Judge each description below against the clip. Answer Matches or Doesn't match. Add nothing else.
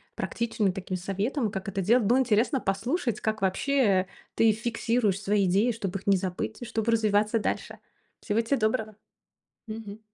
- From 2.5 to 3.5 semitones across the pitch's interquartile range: Matches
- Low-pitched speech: Doesn't match